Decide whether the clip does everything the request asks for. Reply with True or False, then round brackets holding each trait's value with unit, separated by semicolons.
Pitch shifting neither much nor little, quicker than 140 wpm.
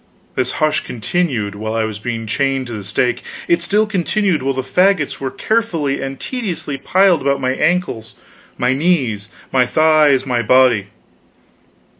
False (5.9 semitones; 155 wpm)